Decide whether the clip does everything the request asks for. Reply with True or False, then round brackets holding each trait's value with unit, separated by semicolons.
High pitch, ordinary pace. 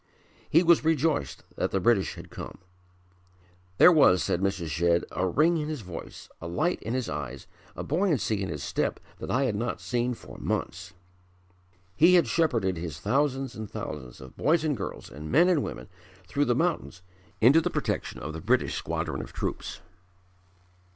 False (120 Hz; 180 wpm)